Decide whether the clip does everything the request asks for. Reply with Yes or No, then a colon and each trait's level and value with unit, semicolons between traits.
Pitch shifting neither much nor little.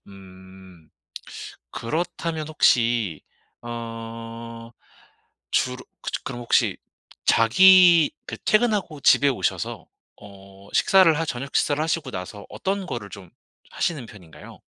No: wide, 7.8 semitones